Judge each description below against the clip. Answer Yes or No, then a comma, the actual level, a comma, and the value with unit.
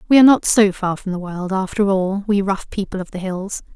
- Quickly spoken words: Yes, fast, 255 wpm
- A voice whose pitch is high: Yes, high, 195 Hz